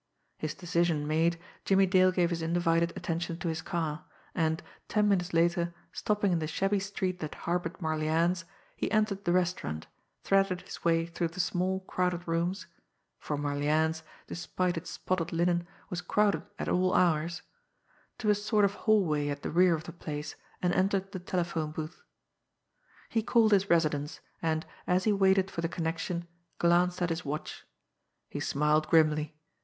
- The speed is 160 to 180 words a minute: Yes, average, 165 wpm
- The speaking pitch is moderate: Yes, medium, 175 Hz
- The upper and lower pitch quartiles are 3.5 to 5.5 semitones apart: No, narrow, 2.4 semitones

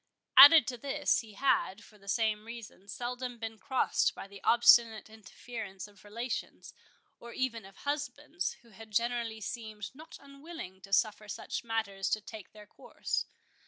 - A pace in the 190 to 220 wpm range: No, average, 160 wpm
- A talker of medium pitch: No, high, 225 Hz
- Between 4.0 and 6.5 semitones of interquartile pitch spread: No, average, 3.0 semitones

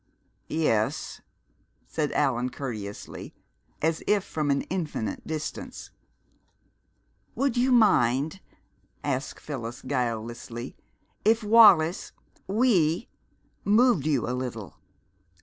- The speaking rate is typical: No, slow, 90 wpm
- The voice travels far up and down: Yes, wide, 8.4 semitones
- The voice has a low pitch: No, medium, 150 Hz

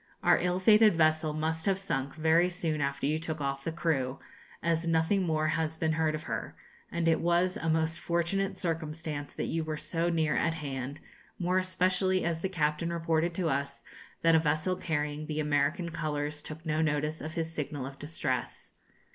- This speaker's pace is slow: No, average, 190 wpm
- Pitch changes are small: Yes, narrow, 2.0 semitones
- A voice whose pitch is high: No, medium, 160 Hz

